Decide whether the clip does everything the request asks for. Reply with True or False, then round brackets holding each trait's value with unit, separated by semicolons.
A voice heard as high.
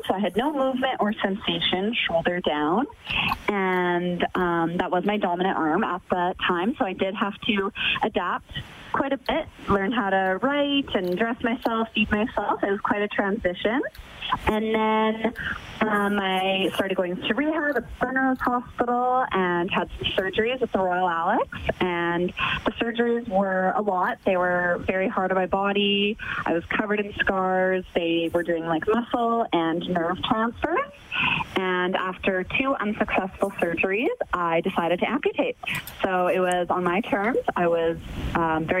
True (195 Hz)